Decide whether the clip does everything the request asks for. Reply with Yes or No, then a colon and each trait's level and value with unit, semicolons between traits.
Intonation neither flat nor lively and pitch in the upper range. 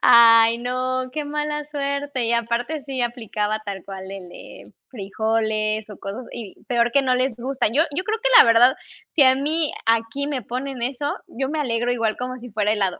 Yes: average, 3.5 semitones; high, 245 Hz